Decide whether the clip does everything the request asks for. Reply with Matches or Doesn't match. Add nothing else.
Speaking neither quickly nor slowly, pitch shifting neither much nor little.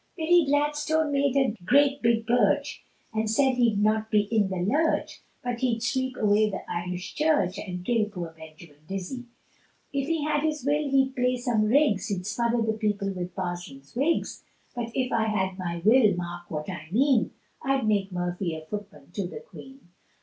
Doesn't match